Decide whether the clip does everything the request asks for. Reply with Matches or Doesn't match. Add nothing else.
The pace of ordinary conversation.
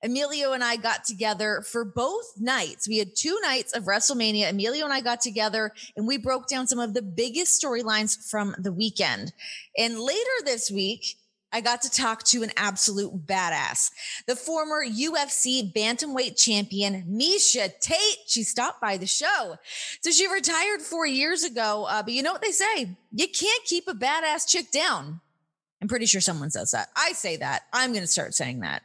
Matches